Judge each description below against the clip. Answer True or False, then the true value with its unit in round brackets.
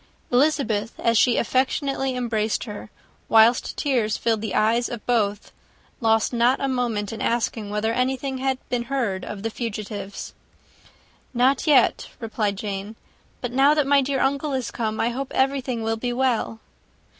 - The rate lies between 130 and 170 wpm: True (155 wpm)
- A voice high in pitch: True (235 Hz)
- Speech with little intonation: False (3.3 semitones)